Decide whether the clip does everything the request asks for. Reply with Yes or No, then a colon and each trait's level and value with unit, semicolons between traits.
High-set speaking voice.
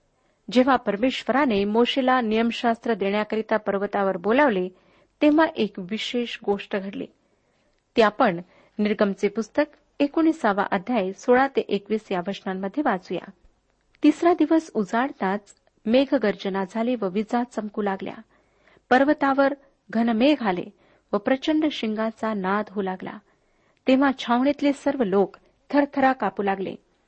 Yes: high, 220 Hz